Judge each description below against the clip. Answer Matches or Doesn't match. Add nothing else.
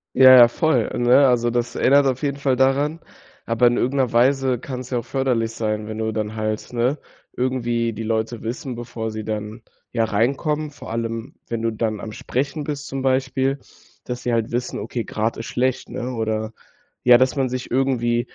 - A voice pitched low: Matches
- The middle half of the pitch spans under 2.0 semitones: Doesn't match